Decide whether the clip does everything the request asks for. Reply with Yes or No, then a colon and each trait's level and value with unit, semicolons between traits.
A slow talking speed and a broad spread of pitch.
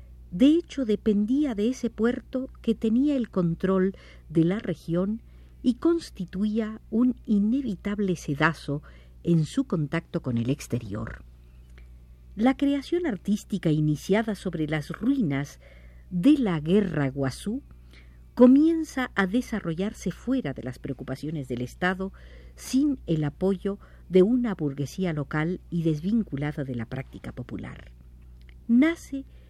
Yes: slow, 120 wpm; wide, 8.5 semitones